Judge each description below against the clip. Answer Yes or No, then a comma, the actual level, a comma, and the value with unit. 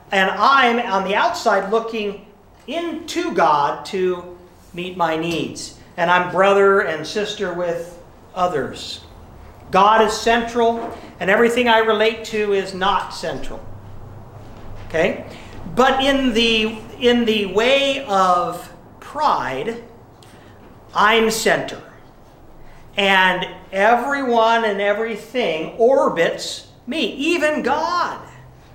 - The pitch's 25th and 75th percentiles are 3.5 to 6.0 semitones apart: Yes, average, 4.6 semitones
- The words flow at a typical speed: No, slow, 100 wpm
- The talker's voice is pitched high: Yes, high, 205 Hz